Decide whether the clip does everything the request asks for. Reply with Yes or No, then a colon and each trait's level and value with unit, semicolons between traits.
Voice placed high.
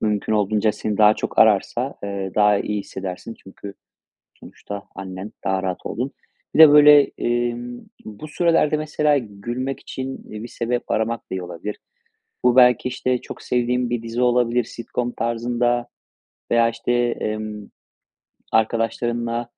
No: low, 115 Hz